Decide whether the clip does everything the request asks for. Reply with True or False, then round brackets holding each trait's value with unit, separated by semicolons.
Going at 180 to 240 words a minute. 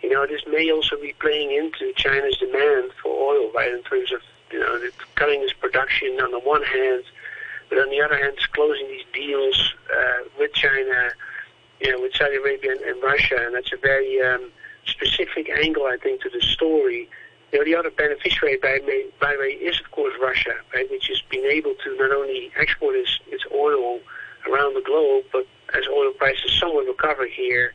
True (200 wpm)